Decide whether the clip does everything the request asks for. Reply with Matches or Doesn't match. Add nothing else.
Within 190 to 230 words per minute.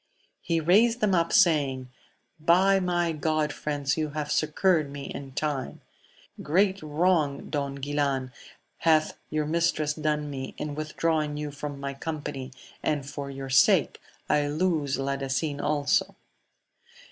Doesn't match